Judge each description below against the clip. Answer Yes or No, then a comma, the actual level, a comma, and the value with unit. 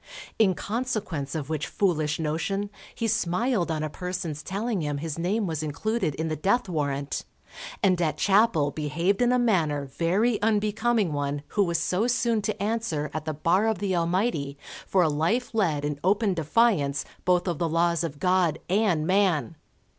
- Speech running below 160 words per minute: No, average, 175 wpm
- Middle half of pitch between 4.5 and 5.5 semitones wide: Yes, average, 5.2 semitones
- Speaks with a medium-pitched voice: Yes, medium, 175 Hz